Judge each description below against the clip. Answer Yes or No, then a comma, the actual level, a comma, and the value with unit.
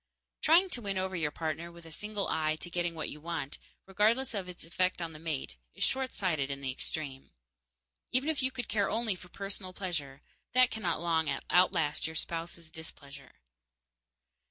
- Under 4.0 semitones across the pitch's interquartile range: No, average, 4.3 semitones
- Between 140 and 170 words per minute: No, average, 180 wpm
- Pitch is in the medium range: Yes, medium, 170 Hz